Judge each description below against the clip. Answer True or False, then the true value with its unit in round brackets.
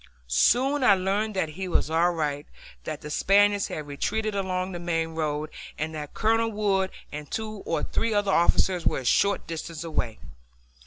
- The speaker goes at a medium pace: True (175 wpm)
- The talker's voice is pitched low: False (185 Hz)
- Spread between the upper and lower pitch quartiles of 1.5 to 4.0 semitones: False (4.7 semitones)